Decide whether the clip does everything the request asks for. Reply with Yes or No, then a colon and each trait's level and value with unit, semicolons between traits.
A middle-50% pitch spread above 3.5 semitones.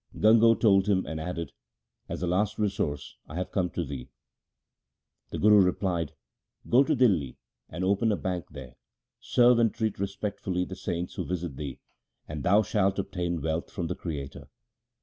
Yes: average, 4.1 semitones